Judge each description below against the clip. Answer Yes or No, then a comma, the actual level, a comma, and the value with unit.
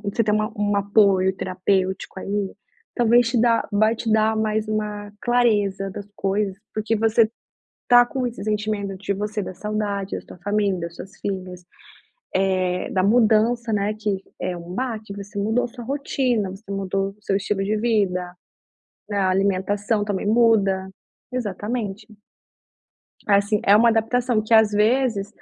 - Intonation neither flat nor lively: No, narrow, 2.3 semitones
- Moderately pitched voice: No, high, 210 Hz